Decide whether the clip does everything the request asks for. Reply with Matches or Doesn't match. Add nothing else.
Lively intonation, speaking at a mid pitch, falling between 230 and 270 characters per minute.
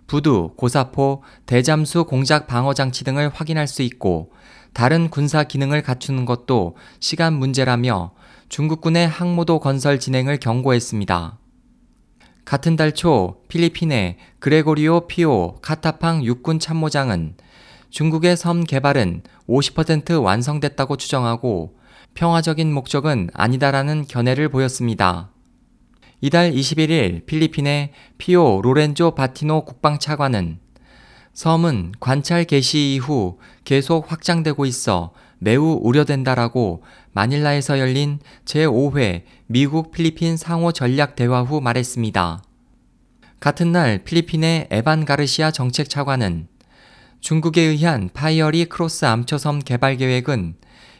Doesn't match